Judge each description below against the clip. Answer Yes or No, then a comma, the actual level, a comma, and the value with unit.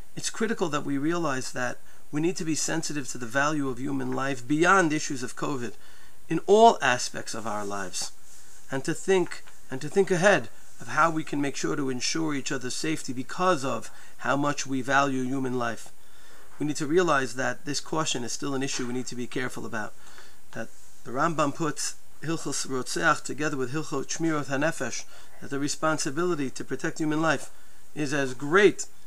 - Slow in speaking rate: No, average, 190 wpm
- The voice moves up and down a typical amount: Yes, average, 3.4 semitones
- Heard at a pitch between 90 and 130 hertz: No, medium, 140 Hz